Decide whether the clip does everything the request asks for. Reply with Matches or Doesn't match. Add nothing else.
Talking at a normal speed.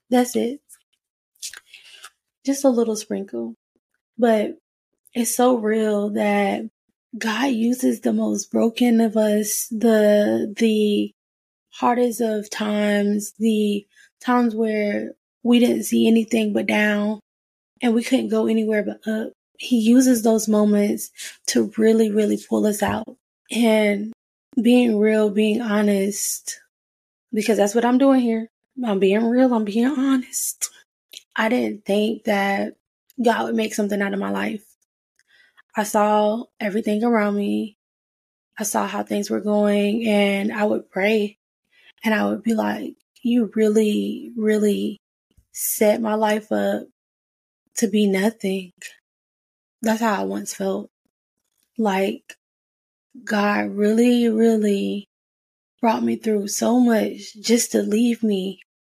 Doesn't match